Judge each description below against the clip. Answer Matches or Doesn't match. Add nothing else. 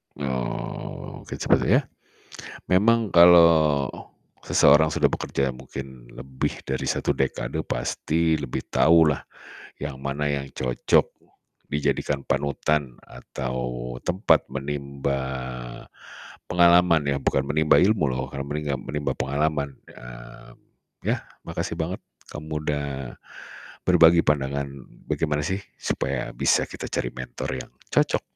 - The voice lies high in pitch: Doesn't match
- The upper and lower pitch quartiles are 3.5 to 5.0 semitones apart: Doesn't match